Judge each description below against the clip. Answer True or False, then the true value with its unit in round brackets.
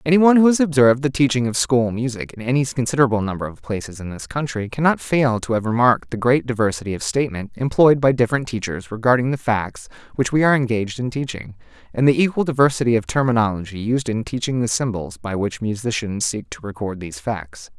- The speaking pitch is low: True (120 Hz)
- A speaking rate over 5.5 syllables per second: True (6.3 syllables/s)